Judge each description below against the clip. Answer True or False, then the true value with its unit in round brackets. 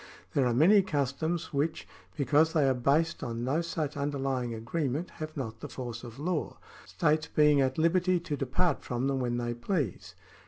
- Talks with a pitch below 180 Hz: True (140 Hz)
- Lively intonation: False (4.3 semitones)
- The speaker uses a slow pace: False (185 wpm)